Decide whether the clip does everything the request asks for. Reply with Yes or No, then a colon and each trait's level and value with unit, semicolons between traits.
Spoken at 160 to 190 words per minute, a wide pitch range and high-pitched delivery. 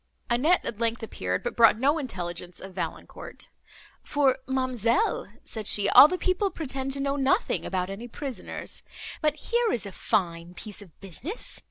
Yes: average, 165 wpm; wide, 6.7 semitones; high, 240 Hz